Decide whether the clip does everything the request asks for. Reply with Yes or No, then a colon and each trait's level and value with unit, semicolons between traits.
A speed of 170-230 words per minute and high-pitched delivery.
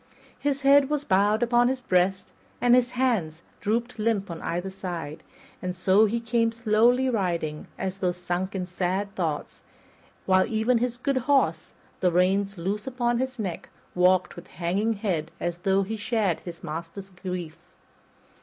No: average, 160 wpm; high, 195 Hz